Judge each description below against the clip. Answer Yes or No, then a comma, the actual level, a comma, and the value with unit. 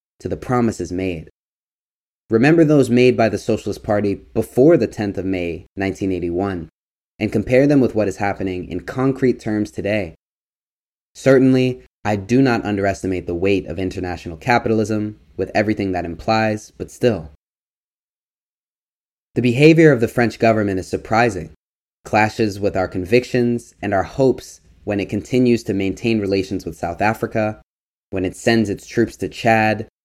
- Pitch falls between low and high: No, low, 105 Hz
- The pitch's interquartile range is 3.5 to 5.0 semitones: Yes, average, 4.0 semitones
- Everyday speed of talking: Yes, average, 150 wpm